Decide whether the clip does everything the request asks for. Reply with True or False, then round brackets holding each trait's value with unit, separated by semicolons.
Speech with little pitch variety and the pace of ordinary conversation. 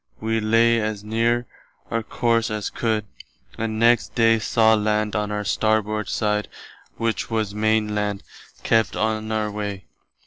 True (1.2 semitones; 150 wpm)